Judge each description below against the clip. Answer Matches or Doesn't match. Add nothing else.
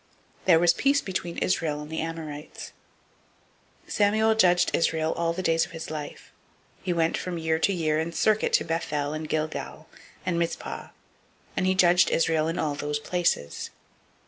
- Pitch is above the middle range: Doesn't match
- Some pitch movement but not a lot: Doesn't match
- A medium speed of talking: Matches